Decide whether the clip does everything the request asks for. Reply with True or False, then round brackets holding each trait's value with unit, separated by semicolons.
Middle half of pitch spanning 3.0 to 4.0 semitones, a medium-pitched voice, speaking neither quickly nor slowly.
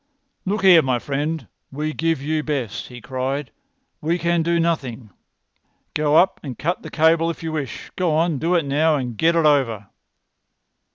True (3.6 semitones; 155 Hz; 170 wpm)